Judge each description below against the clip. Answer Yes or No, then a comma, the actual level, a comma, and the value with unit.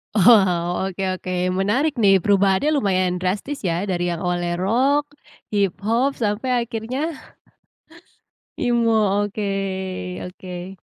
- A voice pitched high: Yes, high, 200 Hz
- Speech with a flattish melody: No, average, 4.1 semitones